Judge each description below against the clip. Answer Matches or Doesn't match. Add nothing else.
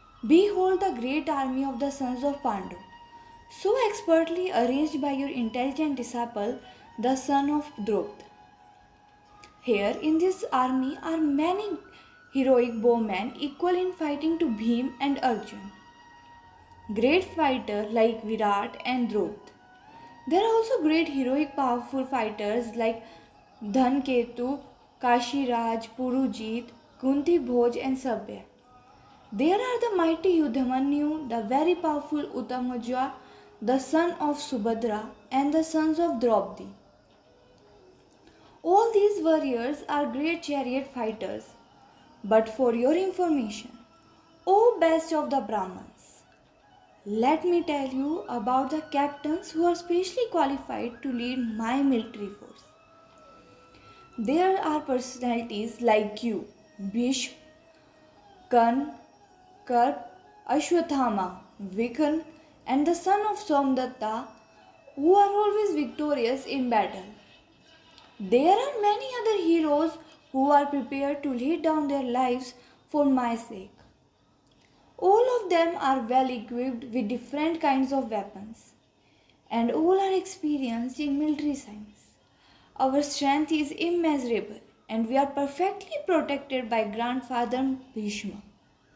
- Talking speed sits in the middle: Matches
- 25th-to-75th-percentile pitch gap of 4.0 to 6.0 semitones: Matches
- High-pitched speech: Matches